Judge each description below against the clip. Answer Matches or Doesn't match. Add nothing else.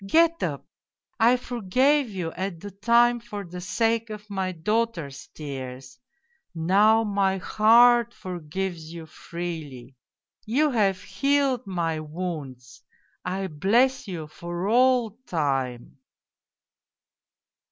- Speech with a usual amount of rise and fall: Doesn't match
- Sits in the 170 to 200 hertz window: Matches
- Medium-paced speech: Doesn't match